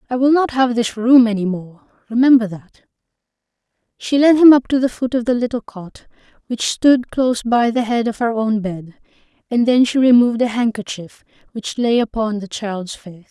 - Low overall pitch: No, high, 230 Hz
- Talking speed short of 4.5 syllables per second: No, 5.0 syllables/s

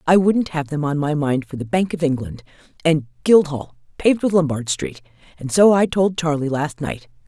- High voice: No, medium, 155 Hz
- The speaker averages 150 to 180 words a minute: No, fast, 205 wpm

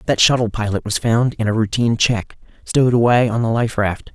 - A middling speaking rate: No, fast, 215 wpm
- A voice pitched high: No, low, 115 Hz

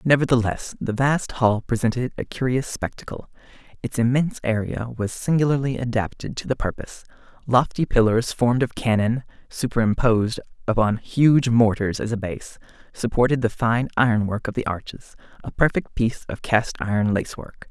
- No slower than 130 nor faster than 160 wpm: Yes, average, 145 wpm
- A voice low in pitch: Yes, low, 120 Hz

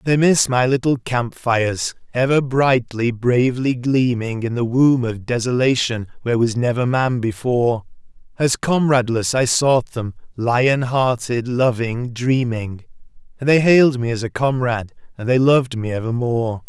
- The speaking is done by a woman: No, male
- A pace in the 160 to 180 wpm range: No, average, 145 wpm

